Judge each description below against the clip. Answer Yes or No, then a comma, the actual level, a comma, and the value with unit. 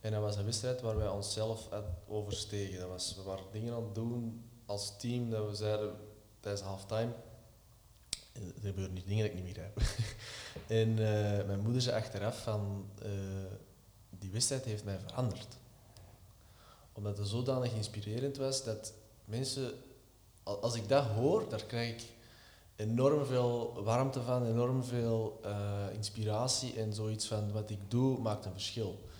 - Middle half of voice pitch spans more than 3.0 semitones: No, narrow, 2.5 semitones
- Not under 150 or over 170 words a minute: Yes, average, 155 wpm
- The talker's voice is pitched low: Yes, low, 110 Hz